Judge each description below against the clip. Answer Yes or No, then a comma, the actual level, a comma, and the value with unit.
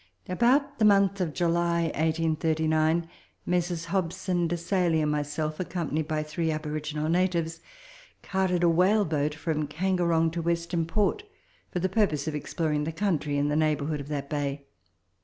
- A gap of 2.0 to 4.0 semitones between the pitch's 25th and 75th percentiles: Yes, average, 2.7 semitones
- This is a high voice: No, medium, 165 Hz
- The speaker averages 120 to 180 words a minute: Yes, average, 155 wpm